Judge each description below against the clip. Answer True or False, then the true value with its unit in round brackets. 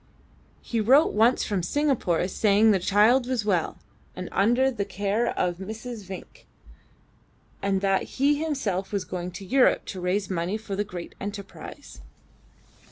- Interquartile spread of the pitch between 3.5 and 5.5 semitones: True (4.0 semitones)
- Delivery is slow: False (155 wpm)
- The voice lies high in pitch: True (205 Hz)